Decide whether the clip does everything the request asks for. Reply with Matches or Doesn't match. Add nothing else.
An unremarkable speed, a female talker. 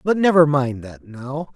Doesn't match